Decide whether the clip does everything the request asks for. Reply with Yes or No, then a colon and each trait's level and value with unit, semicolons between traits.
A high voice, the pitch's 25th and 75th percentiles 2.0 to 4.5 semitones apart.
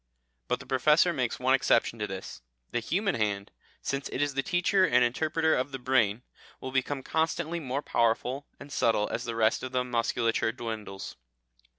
No: low, 130 Hz; average, 4.0 semitones